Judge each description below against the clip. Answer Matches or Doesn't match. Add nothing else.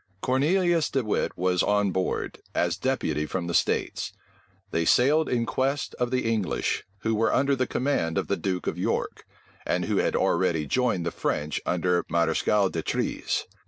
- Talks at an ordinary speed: Matches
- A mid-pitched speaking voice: Doesn't match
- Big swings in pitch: Matches